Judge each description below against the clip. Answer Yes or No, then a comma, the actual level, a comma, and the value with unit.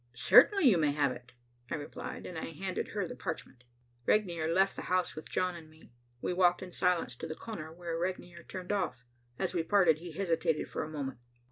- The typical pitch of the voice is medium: Yes, medium, 170 Hz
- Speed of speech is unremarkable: No, fast, 210 wpm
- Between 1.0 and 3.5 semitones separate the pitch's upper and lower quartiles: Yes, average, 2.8 semitones